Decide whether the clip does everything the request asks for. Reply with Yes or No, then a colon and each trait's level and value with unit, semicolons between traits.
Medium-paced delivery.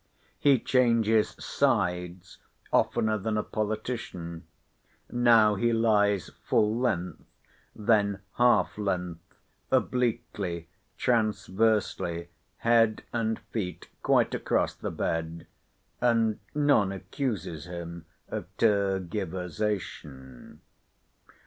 No: slow, 85 wpm